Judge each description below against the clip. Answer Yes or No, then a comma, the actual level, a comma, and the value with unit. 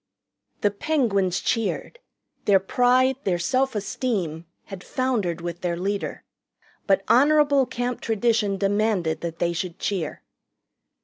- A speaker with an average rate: No, slow, 120 wpm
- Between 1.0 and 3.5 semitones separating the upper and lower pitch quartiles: No, wide, 5.6 semitones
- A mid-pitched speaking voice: No, high, 205 Hz